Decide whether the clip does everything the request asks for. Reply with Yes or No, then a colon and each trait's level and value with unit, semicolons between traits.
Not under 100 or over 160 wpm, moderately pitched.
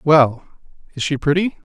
Yes: average, 140 wpm; medium, 155 Hz